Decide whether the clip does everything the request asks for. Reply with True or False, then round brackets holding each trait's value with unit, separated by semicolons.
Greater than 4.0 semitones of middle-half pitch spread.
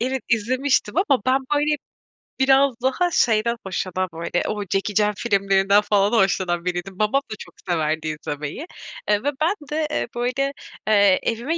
True (5.6 semitones)